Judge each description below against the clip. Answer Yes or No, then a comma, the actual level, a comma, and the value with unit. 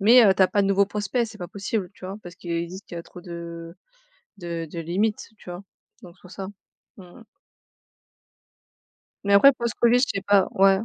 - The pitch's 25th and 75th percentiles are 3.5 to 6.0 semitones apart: No, average, 2.8 semitones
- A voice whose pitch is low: No, high, 195 Hz